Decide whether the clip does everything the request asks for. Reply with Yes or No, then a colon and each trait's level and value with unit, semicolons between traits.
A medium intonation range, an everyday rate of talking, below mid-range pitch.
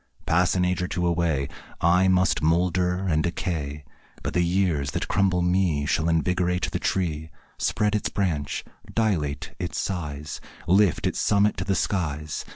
Yes: average, 3.0 semitones; average, 160 wpm; very low, 90 Hz